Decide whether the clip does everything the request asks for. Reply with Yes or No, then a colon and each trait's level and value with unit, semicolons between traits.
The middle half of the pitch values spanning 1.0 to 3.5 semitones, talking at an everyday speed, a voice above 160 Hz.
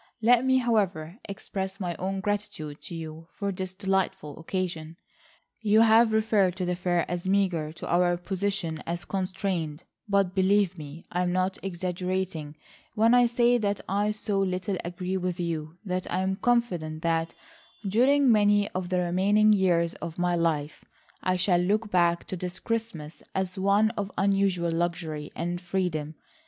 Yes: average, 2.8 semitones; average, 160 wpm; medium, 185 Hz